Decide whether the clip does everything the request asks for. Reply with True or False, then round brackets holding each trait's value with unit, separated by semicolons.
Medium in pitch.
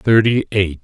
False (105 Hz)